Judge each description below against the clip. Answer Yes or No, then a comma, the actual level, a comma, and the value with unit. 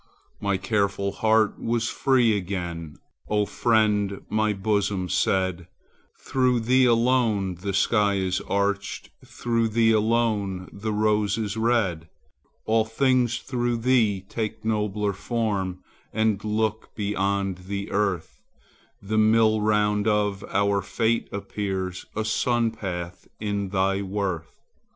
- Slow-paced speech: Yes, slow, 120 wpm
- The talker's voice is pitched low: Yes, low, 105 Hz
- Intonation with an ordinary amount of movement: No, narrow, 2.3 semitones